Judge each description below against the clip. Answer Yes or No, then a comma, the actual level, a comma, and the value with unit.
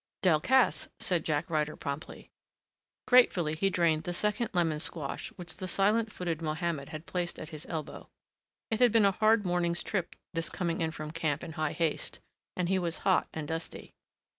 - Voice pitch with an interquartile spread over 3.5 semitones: No, average, 3.2 semitones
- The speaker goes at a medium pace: Yes, average, 180 wpm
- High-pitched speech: No, medium, 170 Hz